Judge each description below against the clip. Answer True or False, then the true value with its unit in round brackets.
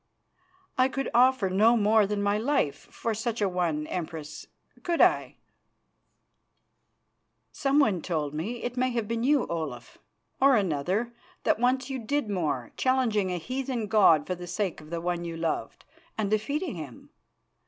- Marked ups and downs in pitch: True (6.6 semitones)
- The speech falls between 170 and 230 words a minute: False (155 wpm)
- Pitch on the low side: False (210 Hz)